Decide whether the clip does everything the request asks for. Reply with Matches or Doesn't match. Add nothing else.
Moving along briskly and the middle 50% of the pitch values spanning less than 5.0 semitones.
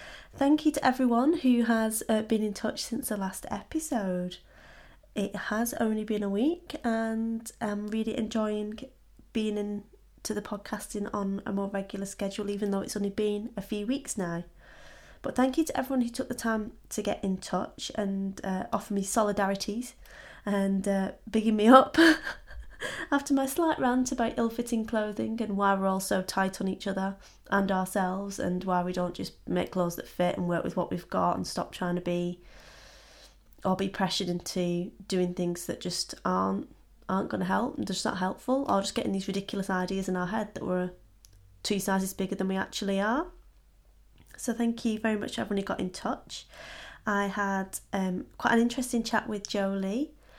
Doesn't match